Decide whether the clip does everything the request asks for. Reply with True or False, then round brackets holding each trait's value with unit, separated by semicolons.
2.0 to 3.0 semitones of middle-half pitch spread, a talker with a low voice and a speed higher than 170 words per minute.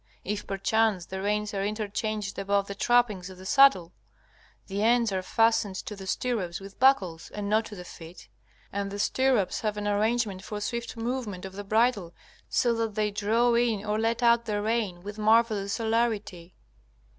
False (2.6 semitones; 210 Hz; 180 wpm)